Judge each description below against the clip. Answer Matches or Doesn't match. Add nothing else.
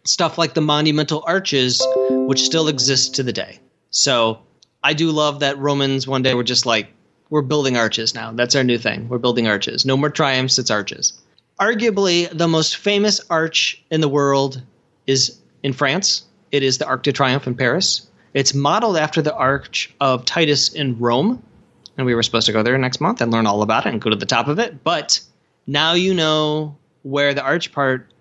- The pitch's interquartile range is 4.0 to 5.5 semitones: Doesn't match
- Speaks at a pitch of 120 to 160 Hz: Matches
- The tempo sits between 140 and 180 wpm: Doesn't match